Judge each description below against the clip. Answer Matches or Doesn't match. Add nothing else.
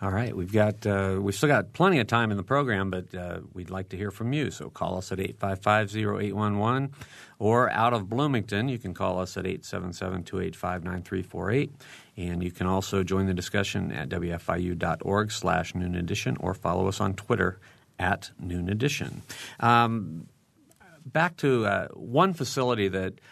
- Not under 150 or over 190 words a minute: Matches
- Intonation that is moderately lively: Matches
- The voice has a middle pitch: Doesn't match